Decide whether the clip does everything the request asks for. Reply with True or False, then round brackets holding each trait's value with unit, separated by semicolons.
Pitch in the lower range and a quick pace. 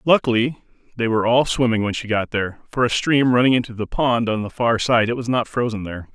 True (115 Hz; 245 wpm)